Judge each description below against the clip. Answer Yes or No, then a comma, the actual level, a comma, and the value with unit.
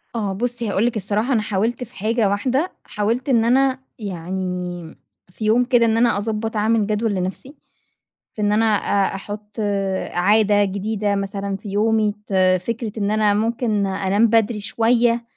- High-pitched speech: Yes, high, 215 Hz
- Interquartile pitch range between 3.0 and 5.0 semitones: No, narrow, 2.4 semitones